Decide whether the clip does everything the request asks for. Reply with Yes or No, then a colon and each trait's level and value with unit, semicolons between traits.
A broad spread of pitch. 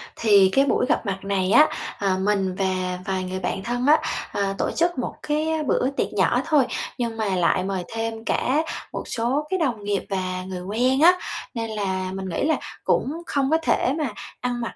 Yes: wide, 6.1 semitones